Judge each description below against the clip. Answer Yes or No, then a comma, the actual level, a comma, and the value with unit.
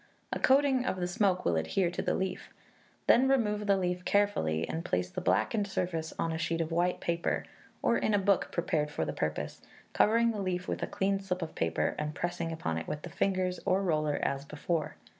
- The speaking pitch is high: No, medium, 180 Hz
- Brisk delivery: Yes, fast, 215 wpm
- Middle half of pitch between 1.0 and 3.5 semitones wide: No, average, 4.3 semitones